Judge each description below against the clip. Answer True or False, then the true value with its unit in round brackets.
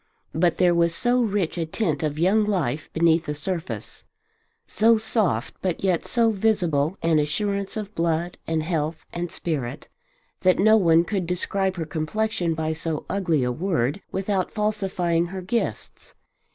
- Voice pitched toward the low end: False (175 Hz)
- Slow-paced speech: False (155 wpm)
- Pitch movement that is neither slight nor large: True (3.8 semitones)